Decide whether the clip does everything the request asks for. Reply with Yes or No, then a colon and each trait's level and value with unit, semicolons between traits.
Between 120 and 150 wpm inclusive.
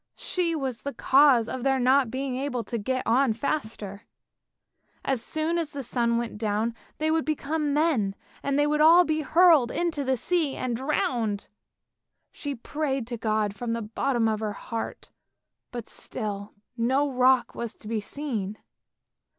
No: average, 165 wpm